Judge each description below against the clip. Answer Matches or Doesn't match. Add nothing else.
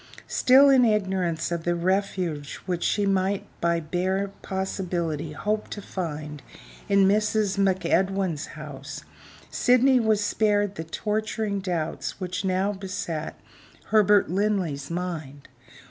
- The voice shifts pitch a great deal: Doesn't match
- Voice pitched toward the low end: Doesn't match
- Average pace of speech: Doesn't match